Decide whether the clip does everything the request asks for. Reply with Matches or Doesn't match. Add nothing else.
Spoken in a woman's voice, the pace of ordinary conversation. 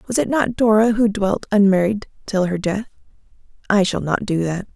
Matches